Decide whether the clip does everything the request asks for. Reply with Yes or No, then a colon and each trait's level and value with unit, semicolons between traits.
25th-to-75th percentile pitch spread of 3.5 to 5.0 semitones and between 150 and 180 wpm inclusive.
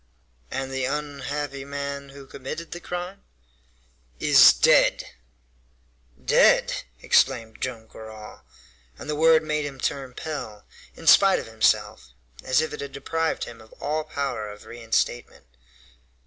No: average, 4.1 semitones; slow, 135 wpm